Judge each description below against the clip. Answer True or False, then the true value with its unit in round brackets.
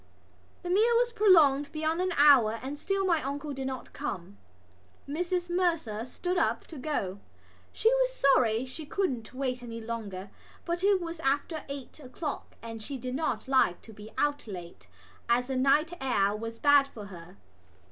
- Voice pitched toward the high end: True (275 Hz)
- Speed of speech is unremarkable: True (170 wpm)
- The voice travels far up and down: True (6.4 semitones)